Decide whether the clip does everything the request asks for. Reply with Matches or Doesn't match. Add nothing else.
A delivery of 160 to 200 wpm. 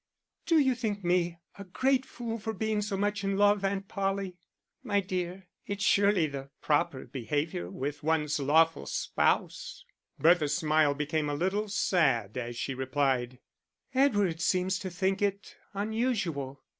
Doesn't match